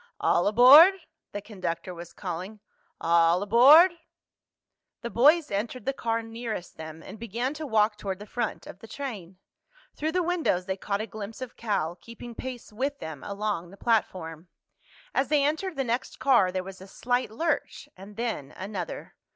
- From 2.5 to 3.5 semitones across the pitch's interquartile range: No, average, 5.3 semitones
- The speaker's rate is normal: Yes, average, 170 wpm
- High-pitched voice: Yes, high, 220 Hz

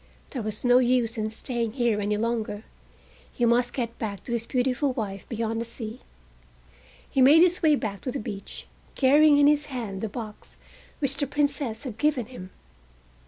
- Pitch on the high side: Yes, high, 240 Hz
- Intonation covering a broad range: No, average, 3.7 semitones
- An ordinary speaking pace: Yes, average, 180 wpm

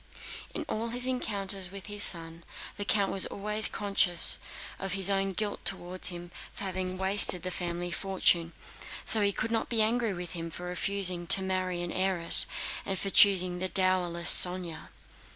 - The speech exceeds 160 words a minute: Yes, average, 170 wpm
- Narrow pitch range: Yes, narrow, 2.2 semitones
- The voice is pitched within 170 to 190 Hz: Yes, medium, 185 Hz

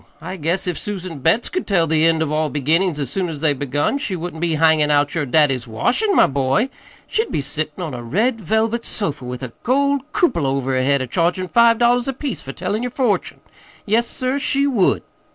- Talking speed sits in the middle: No, fast, 220 wpm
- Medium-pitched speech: Yes, medium, 170 Hz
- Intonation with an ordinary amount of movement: No, wide, 8.2 semitones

